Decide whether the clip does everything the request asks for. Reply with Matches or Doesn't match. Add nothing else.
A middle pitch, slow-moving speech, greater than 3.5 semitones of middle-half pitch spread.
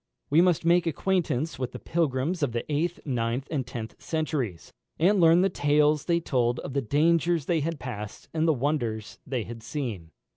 Doesn't match